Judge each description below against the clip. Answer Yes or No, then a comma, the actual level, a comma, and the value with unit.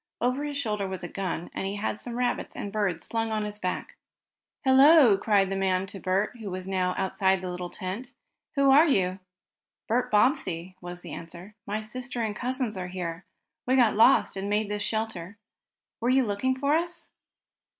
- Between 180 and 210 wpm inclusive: Yes, average, 190 wpm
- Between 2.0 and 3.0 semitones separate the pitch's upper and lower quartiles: No, average, 4.8 semitones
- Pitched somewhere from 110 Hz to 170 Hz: No, high, 210 Hz